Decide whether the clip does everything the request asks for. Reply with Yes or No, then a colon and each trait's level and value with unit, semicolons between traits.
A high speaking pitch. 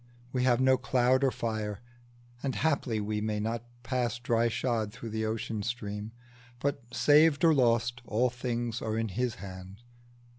No: low, 120 Hz